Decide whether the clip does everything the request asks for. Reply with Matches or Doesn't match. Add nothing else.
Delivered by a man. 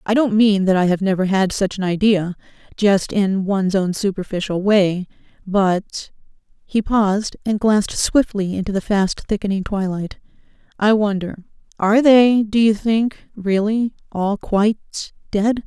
Doesn't match